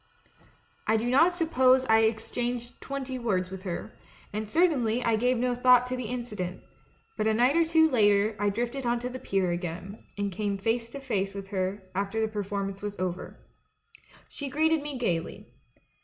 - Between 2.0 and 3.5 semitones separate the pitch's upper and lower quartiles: No, average, 4.1 semitones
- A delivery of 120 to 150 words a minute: No, average, 180 wpm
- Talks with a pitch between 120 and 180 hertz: No, high, 225 Hz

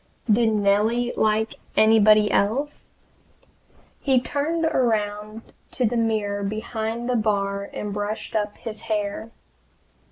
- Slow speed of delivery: Yes, slow, 115 wpm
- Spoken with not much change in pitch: Yes, narrow, 2.2 semitones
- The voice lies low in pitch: No, high, 220 Hz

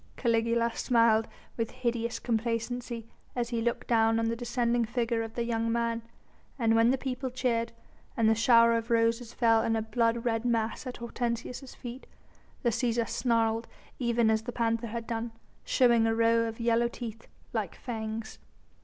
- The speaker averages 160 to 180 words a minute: Yes, average, 170 wpm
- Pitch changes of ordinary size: No, narrow, 0.9 semitones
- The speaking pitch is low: No, high, 230 Hz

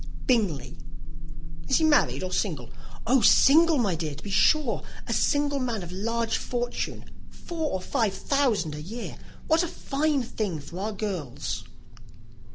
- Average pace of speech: Yes, average, 155 wpm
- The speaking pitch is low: No, high, 225 Hz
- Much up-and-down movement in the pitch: Yes, wide, 7.3 semitones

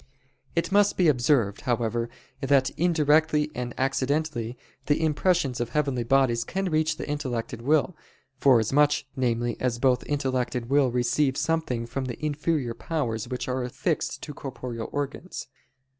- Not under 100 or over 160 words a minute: Yes, average, 145 wpm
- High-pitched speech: No, low, 135 Hz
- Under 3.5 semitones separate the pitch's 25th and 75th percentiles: No, average, 3.9 semitones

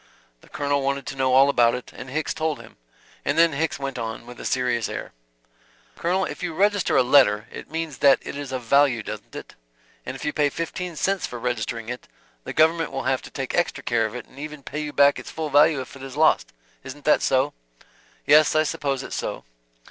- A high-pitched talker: No, medium, 140 Hz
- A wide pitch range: No, average, 3.6 semitones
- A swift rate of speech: Yes, fast, 225 wpm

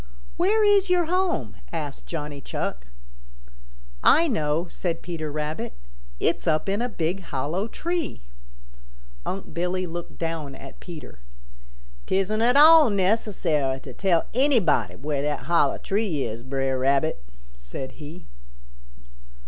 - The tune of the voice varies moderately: No, wide, 6.9 semitones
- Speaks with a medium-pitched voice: Yes, medium, 170 Hz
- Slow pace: Yes, slow, 125 wpm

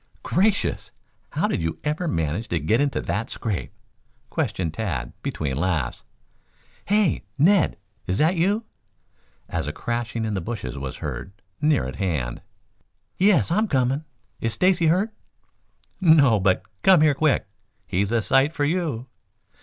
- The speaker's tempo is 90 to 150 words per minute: Yes, average, 145 wpm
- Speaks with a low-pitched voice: Yes, low, 120 Hz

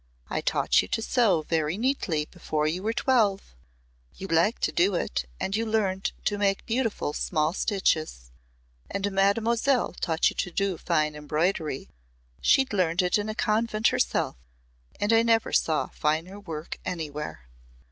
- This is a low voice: No, high, 190 Hz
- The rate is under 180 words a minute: Yes, average, 155 wpm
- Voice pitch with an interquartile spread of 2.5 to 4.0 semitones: No, wide, 5.4 semitones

